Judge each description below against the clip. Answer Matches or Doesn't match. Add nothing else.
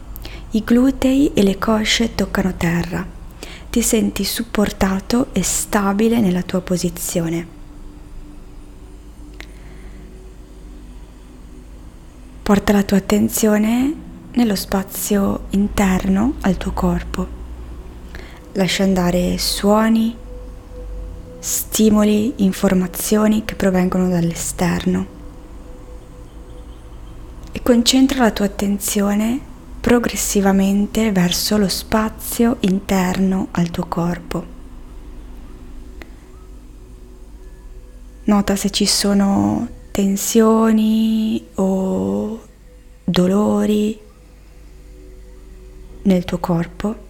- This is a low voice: Doesn't match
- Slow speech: Matches